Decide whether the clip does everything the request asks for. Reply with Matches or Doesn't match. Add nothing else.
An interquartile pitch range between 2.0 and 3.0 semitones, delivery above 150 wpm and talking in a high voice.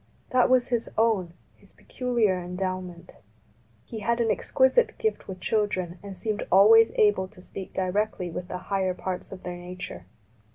Doesn't match